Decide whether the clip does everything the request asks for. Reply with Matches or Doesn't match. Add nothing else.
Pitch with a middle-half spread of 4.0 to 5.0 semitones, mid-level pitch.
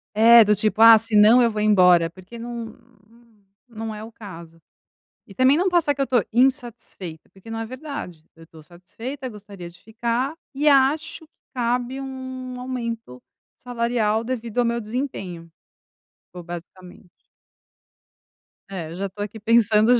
Doesn't match